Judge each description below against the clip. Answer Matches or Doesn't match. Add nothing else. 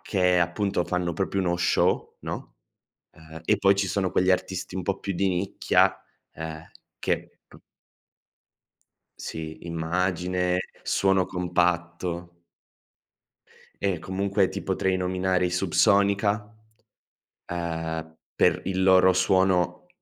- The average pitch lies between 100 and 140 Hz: Doesn't match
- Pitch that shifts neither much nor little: Doesn't match